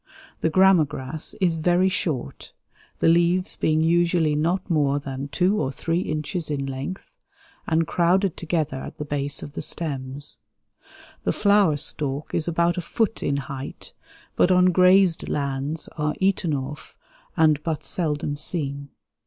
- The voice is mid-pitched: Yes, medium, 160 Hz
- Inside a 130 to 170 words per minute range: Yes, average, 150 wpm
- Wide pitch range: No, average, 3.7 semitones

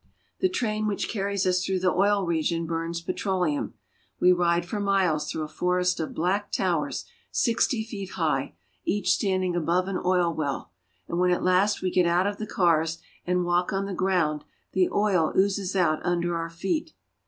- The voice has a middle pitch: Yes, medium, 180 Hz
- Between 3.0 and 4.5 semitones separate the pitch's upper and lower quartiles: No, narrow, 2.6 semitones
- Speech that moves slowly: No, average, 180 wpm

